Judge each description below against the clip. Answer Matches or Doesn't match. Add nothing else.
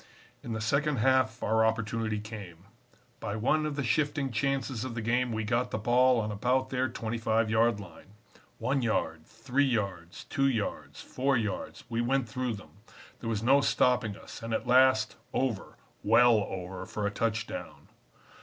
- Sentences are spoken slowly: Doesn't match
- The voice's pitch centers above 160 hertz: Doesn't match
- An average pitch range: Matches